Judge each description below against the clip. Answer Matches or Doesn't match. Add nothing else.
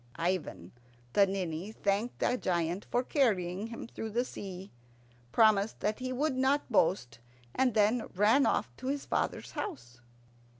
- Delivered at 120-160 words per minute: Matches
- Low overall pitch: Doesn't match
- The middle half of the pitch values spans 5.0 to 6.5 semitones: Matches